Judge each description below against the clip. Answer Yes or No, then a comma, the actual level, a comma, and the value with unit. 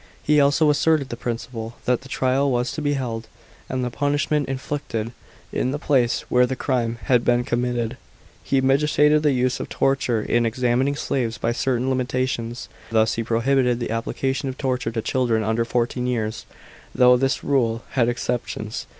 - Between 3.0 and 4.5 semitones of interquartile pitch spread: No, narrow, 2.5 semitones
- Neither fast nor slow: Yes, average, 170 wpm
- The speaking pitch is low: Yes, low, 125 Hz